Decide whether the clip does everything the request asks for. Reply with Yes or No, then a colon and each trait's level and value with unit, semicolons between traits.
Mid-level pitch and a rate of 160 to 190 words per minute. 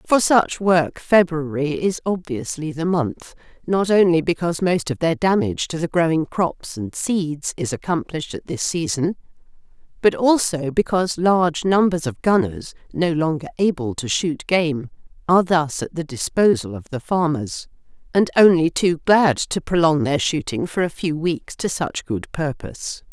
Yes: medium, 165 Hz; average, 165 wpm